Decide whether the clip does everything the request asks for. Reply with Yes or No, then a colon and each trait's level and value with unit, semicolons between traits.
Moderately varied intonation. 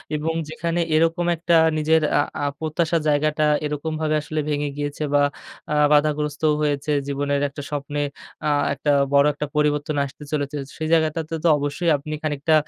No: narrow, 1.5 semitones